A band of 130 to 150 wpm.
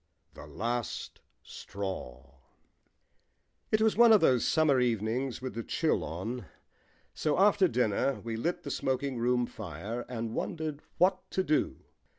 Yes: average, 140 wpm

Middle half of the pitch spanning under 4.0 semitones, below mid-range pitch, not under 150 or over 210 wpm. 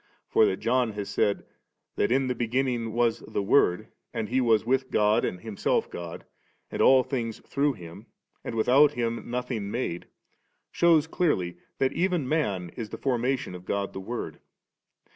No: average, 4.5 semitones; low, 120 Hz; average, 160 wpm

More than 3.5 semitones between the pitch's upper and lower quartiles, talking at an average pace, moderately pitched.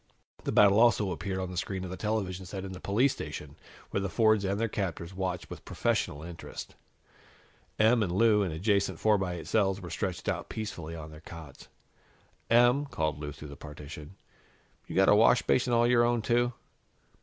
No: average, 4.3 semitones; average, 190 wpm; very low, 95 Hz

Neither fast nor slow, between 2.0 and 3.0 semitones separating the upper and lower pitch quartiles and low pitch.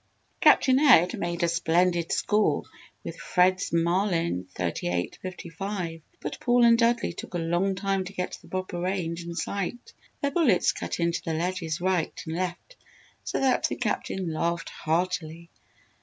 No: average, 155 wpm; narrow, 2.6 semitones; medium, 180 Hz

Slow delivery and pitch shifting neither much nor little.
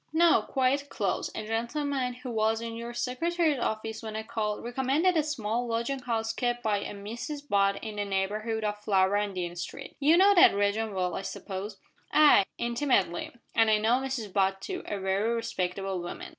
No: average, 185 wpm; average, 4.0 semitones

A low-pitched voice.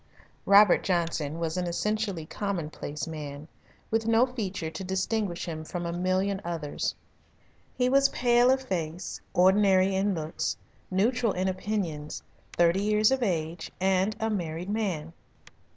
No: medium, 185 Hz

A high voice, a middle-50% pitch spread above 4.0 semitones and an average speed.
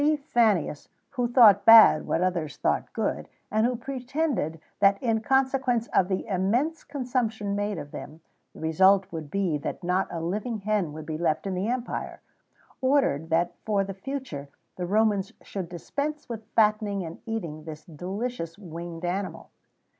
Yes: high, 200 Hz; wide, 5.6 semitones; average, 160 wpm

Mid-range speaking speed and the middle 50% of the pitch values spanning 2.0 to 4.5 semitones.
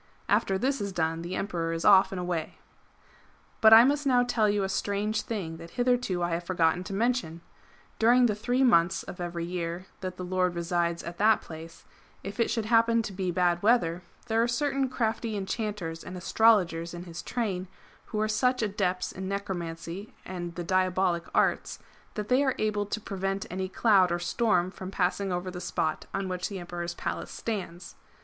Yes: average, 190 wpm; average, 4.0 semitones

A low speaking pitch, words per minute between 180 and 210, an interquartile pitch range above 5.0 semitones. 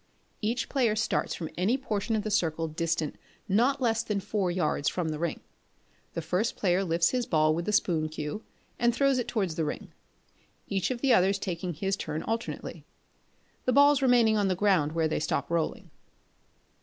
No: high, 195 Hz; average, 185 wpm; wide, 5.5 semitones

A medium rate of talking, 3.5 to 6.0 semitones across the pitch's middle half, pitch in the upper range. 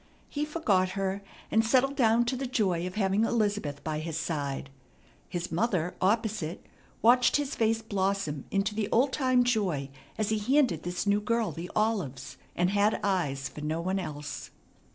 Yes: average, 170 wpm; average, 5.2 semitones; high, 200 Hz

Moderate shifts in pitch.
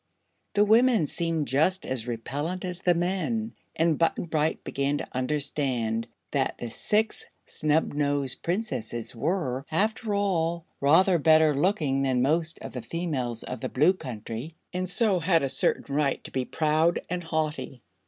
Yes: average, 4.9 semitones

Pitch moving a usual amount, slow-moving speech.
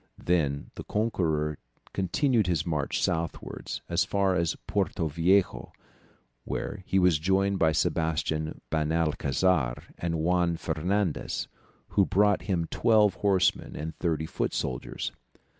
Yes: average, 3.5 semitones; slow, 120 wpm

